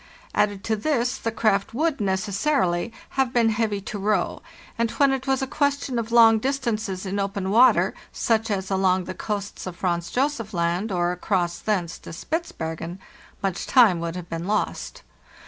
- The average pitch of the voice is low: No, high, 210 Hz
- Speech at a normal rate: Yes, average, 170 wpm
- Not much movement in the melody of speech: No, average, 4.3 semitones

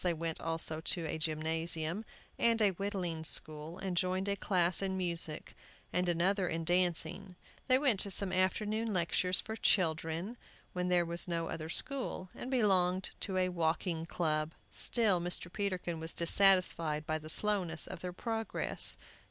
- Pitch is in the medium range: Yes, medium, 180 Hz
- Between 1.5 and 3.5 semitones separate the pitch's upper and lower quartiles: Yes, average, 3.0 semitones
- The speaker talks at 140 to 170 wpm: Yes, average, 160 wpm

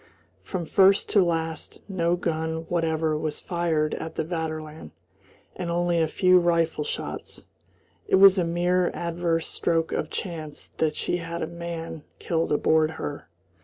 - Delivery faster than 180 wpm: No, average, 150 wpm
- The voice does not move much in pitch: Yes, narrow, 1.5 semitones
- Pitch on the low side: No, medium, 165 Hz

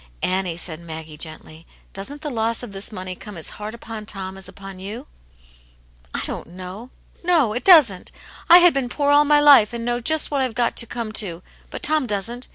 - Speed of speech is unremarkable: No, fast, 215 wpm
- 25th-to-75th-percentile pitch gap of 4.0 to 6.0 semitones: Yes, wide, 5.6 semitones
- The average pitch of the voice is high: Yes, high, 215 Hz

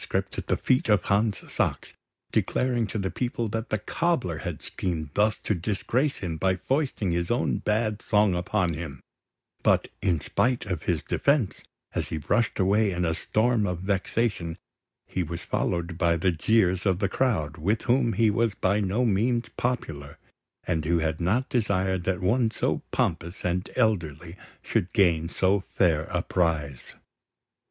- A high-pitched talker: No, very low, 95 Hz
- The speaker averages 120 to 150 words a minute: No, average, 165 wpm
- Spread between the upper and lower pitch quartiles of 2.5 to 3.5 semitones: No, average, 4.7 semitones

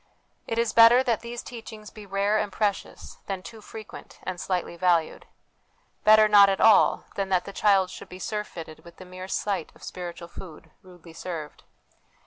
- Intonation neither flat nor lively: Yes, average, 3.1 semitones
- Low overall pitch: No, high, 195 Hz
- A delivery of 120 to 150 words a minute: No, average, 175 wpm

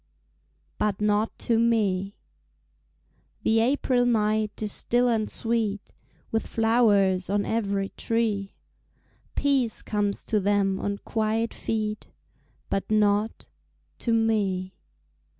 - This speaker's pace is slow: Yes, slow, 105 wpm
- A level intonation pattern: Yes, narrow, 2.0 semitones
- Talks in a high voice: Yes, high, 215 Hz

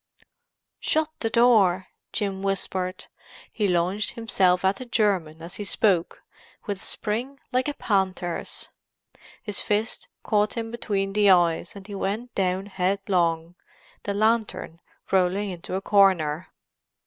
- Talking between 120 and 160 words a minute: Yes, slow, 135 wpm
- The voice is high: Yes, high, 195 Hz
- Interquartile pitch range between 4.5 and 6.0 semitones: No, average, 2.7 semitones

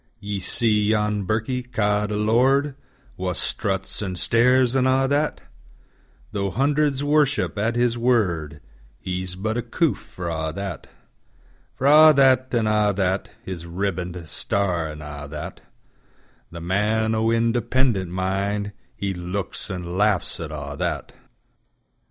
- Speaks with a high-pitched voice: No, low, 105 Hz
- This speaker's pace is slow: Yes, slow, 120 wpm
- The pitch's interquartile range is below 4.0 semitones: No, average, 4.9 semitones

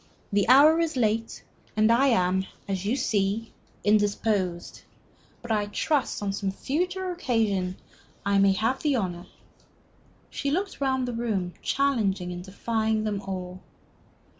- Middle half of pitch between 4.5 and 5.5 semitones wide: Yes, average, 5.0 semitones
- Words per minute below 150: Yes, average, 140 wpm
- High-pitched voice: Yes, high, 215 Hz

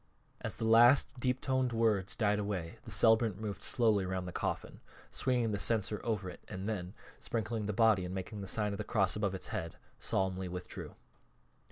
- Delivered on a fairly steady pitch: No, average, 3.2 semitones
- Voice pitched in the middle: No, low, 105 Hz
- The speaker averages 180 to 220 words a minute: Yes, average, 190 wpm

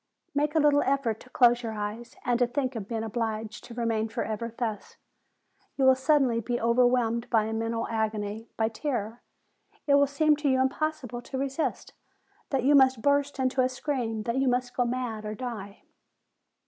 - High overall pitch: Yes, high, 245 Hz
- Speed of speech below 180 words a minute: No, average, 185 wpm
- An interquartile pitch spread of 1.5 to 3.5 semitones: Yes, average, 3.0 semitones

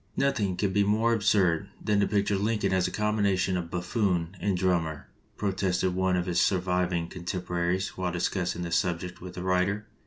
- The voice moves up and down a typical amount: No, narrow, 2.2 semitones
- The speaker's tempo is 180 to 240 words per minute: Yes, average, 185 wpm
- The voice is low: Yes, very low, 95 Hz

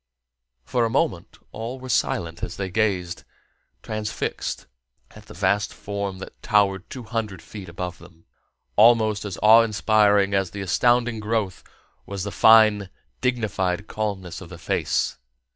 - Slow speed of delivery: No, average, 145 wpm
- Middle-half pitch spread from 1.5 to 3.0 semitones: Yes, average, 2.7 semitones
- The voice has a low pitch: Yes, low, 105 Hz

